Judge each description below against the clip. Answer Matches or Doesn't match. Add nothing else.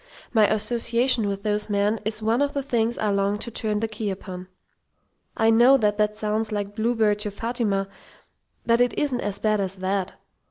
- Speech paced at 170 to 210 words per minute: Matches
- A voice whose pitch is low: Doesn't match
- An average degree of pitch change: Doesn't match